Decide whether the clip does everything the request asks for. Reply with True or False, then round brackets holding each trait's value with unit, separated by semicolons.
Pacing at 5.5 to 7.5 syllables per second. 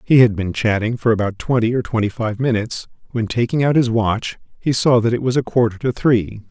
True (5.6 syllables/s)